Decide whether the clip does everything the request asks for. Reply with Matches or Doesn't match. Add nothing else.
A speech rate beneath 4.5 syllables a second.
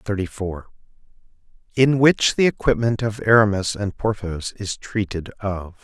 Matches